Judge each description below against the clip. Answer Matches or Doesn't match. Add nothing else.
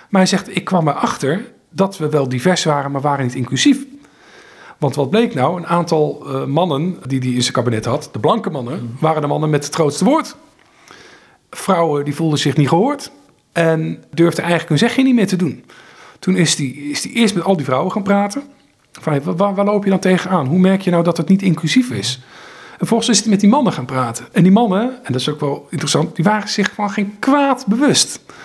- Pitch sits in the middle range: Matches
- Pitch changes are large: Matches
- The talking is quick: Matches